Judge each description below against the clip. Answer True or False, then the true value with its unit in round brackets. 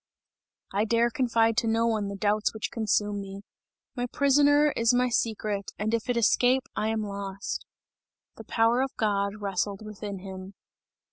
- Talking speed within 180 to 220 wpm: False (155 wpm)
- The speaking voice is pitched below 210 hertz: False (220 Hz)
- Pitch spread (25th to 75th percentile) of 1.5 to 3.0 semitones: True (2.7 semitones)